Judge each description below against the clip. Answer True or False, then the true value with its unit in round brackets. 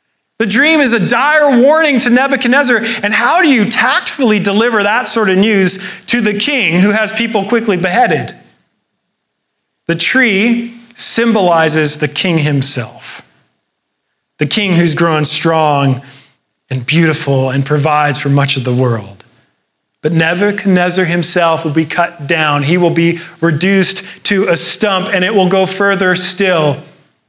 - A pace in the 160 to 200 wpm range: False (145 wpm)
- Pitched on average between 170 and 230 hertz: True (185 Hz)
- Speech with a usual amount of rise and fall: False (6.1 semitones)